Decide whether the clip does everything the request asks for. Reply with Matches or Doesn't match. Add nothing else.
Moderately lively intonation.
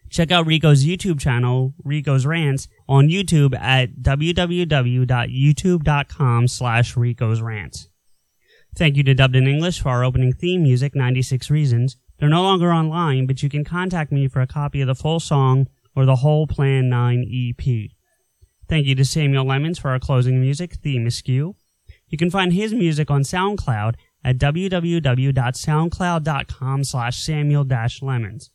Matches